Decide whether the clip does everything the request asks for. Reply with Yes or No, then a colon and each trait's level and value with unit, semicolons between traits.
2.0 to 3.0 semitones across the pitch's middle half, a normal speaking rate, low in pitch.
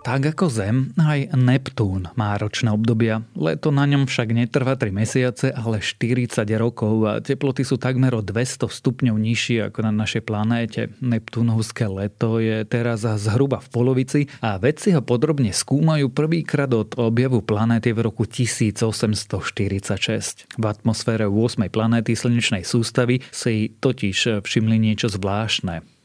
Yes: average, 2.7 semitones; average, 140 wpm; low, 115 Hz